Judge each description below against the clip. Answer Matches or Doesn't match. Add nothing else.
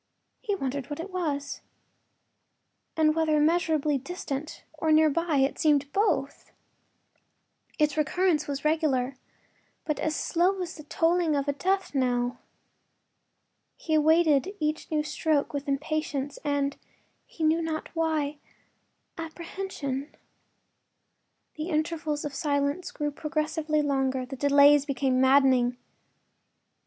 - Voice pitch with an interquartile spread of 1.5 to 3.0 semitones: Matches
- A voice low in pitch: Doesn't match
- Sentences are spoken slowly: Matches